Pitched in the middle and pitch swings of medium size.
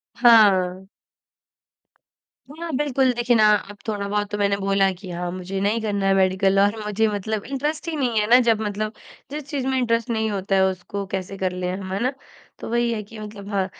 No: high, 210 Hz; average, 3.3 semitones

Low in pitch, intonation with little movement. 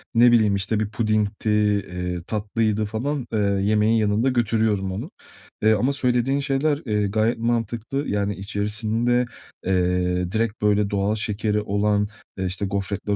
Yes: low, 105 Hz; narrow, 2.2 semitones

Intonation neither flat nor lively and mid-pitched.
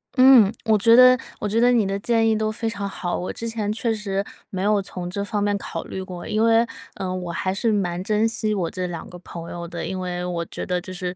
No: average, 3.6 semitones; high, 200 Hz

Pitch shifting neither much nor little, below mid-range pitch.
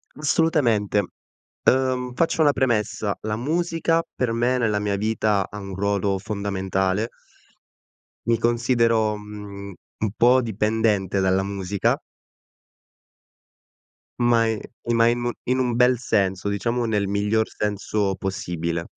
Yes: average, 3.2 semitones; low, 110 Hz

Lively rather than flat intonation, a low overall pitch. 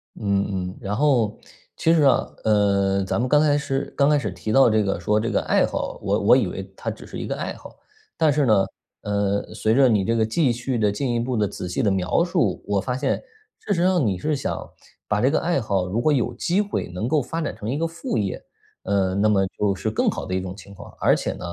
Yes: wide, 5.8 semitones; low, 110 Hz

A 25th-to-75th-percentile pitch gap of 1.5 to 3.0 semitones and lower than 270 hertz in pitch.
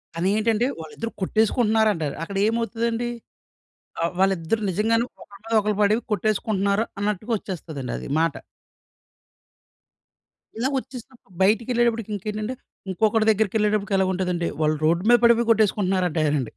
No: average, 3.5 semitones; high, 210 Hz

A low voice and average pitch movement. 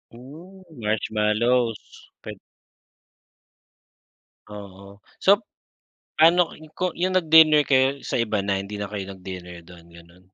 No: low, 110 Hz; wide, 8.5 semitones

